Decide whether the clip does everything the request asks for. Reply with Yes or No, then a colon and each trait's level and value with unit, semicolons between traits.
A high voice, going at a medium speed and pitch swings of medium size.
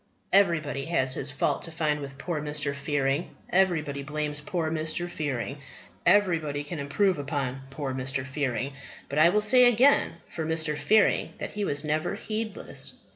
No: medium, 150 Hz; average, 160 wpm; average, 3.7 semitones